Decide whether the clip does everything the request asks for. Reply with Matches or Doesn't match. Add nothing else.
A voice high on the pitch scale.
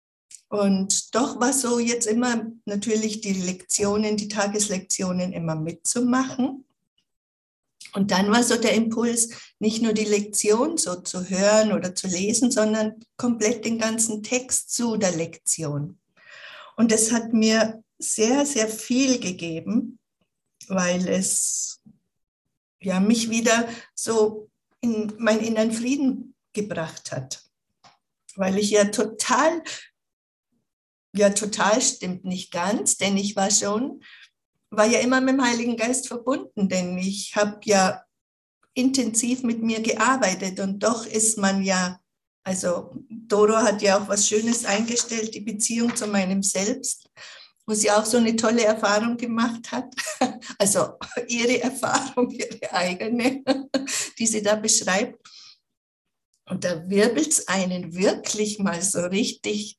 Matches